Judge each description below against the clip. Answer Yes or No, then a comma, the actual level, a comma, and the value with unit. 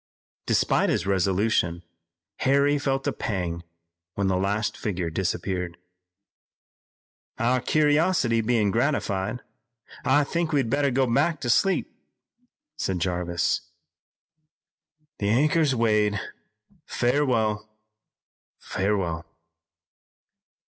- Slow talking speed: Yes, slow, 90 wpm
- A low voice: Yes, low, 110 Hz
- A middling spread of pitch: No, wide, 6.1 semitones